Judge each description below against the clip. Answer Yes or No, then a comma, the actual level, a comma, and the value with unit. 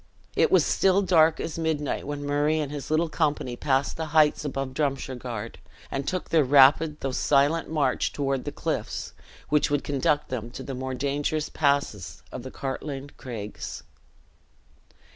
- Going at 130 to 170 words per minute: Yes, average, 160 wpm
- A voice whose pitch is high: No, medium, 145 Hz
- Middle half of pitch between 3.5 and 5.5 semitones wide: No, narrow, 2.5 semitones